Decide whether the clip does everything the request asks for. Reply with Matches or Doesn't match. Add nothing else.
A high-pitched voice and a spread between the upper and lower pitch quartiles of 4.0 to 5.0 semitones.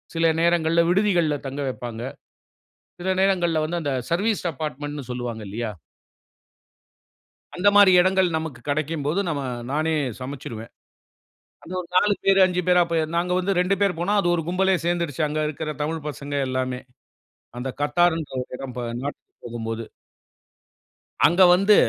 Doesn't match